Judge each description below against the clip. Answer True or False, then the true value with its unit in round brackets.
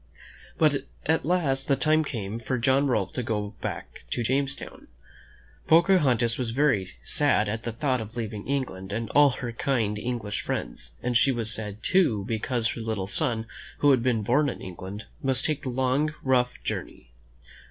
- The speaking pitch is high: False (125 Hz)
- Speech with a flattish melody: False (4.0 semitones)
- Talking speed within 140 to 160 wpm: False (175 wpm)